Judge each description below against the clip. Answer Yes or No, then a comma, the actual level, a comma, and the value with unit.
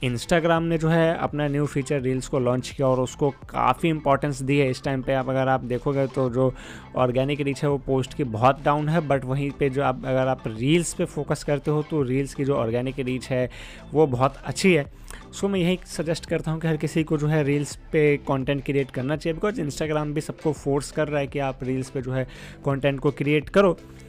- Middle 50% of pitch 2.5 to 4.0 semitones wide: Yes, average, 2.8 semitones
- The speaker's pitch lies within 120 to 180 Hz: Yes, medium, 140 Hz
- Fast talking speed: Yes, fast, 235 wpm